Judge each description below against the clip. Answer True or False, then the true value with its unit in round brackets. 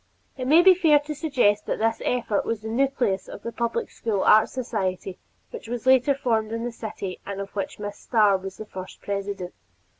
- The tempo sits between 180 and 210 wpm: True (205 wpm)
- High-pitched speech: True (225 Hz)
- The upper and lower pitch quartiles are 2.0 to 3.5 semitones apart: False (4.2 semitones)